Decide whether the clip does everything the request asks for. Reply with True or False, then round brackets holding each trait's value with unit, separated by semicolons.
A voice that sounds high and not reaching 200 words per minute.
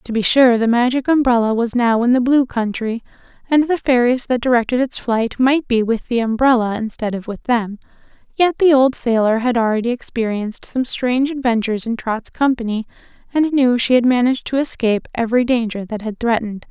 True (240 Hz; 190 wpm)